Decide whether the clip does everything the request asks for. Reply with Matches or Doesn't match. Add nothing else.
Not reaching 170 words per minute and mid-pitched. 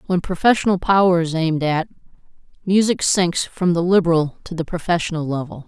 Matches